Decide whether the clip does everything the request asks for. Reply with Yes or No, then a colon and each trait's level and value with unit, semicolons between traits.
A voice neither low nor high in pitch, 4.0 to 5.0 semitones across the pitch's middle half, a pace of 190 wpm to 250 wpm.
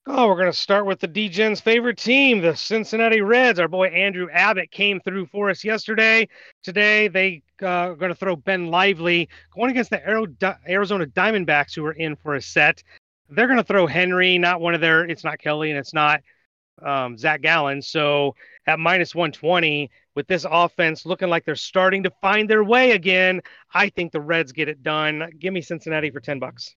Yes: medium, 180 Hz; average, 4.3 semitones; average, 200 wpm